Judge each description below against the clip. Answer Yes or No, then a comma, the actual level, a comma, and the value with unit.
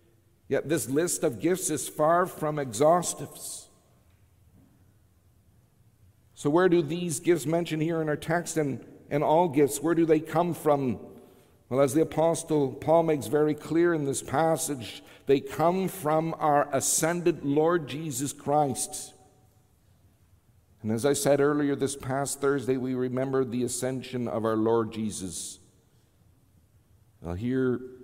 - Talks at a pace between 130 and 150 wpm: Yes, average, 140 wpm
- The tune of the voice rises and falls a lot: Yes, wide, 6.0 semitones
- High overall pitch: No, medium, 140 Hz